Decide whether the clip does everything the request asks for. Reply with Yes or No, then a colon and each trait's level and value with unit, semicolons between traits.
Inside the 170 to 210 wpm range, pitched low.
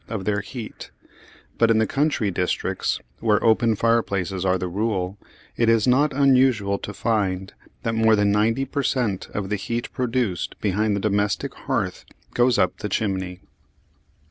No: average, 160 wpm; low, 110 Hz